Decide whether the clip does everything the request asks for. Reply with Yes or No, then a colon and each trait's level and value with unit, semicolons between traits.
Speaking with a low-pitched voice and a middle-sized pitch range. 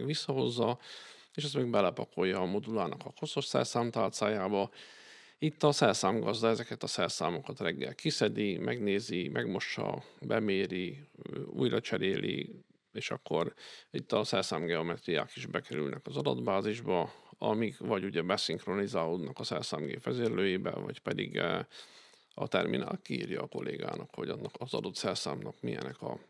No: low, 115 Hz; wide, 6.4 semitones